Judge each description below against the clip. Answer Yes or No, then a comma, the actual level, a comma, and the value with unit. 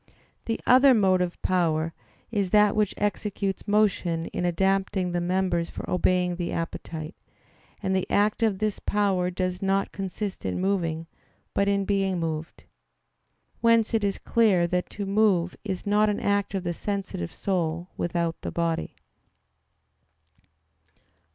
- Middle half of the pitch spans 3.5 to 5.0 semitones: No, average, 2.8 semitones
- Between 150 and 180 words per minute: No, average, 140 wpm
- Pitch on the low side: No, high, 190 Hz